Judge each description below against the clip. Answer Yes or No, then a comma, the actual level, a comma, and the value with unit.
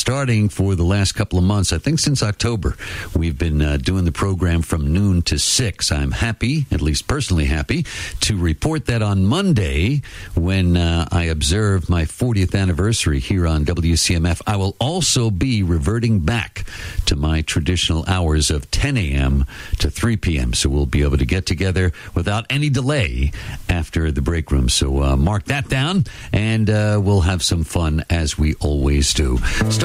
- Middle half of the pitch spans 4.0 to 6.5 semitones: Yes, average, 5.0 semitones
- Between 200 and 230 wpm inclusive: No, average, 175 wpm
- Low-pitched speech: Yes, very low, 90 Hz